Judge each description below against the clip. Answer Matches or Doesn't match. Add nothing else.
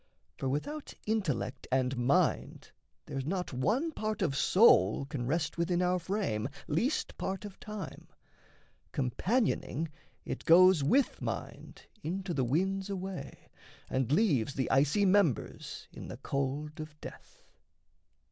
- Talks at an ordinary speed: Doesn't match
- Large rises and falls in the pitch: Matches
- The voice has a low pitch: Doesn't match